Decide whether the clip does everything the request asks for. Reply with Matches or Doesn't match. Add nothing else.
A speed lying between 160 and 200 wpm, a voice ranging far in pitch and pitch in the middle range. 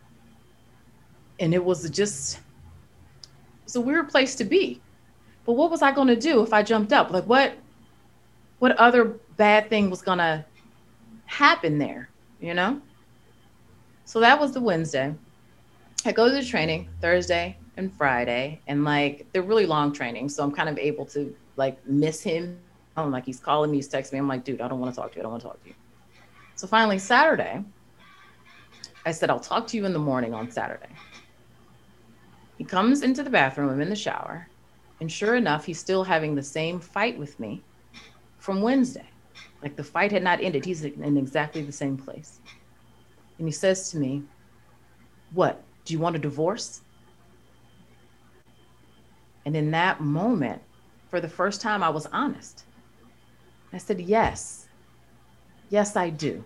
Matches